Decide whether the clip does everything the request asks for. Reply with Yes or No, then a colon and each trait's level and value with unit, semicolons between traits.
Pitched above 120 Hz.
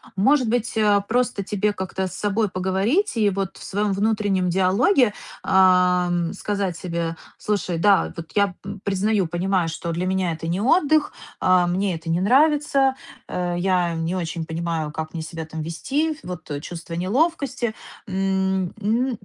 Yes: high, 190 Hz